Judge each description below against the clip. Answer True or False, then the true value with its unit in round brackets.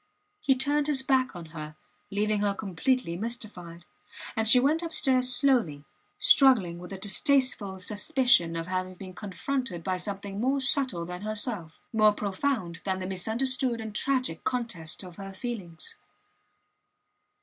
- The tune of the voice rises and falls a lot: True (6.0 semitones)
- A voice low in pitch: False (210 Hz)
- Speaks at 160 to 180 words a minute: False (140 wpm)